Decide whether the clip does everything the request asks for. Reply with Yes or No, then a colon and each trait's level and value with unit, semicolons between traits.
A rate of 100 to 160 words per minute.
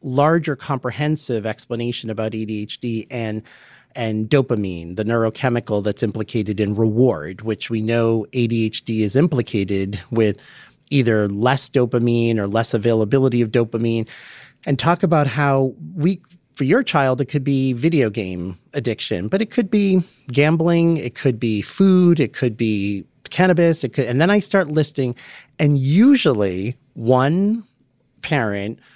Yes: average, 140 wpm